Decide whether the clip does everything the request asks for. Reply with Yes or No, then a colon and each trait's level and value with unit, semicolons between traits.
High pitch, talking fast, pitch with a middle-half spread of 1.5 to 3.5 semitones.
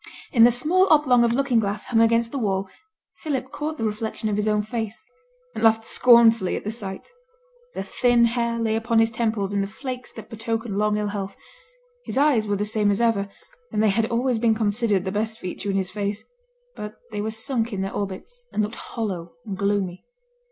Yes: high, 220 Hz; fast, 210 wpm; narrow, 2.5 semitones